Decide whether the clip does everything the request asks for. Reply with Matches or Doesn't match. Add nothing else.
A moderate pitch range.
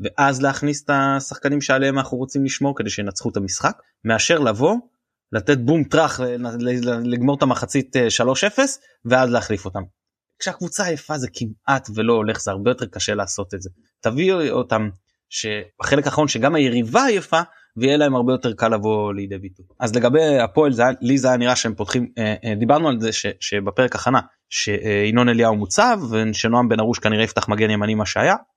Matches